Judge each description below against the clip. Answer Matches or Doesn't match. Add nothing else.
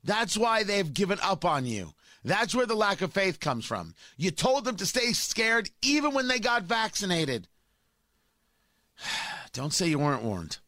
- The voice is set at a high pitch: Matches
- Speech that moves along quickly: Doesn't match